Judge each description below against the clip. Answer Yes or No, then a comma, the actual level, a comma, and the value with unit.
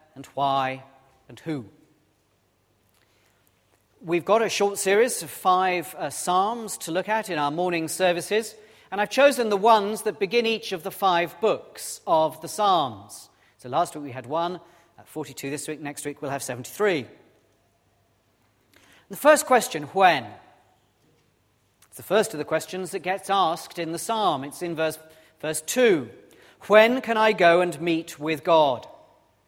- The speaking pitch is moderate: Yes, medium, 165 Hz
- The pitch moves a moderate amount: No, wide, 6.7 semitones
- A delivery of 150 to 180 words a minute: Yes, average, 160 wpm